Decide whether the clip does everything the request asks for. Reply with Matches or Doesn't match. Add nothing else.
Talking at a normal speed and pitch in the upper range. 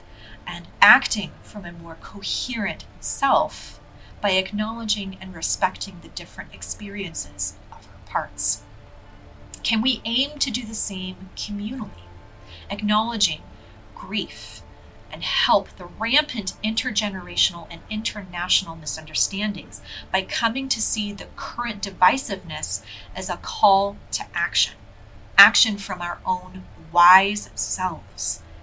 Doesn't match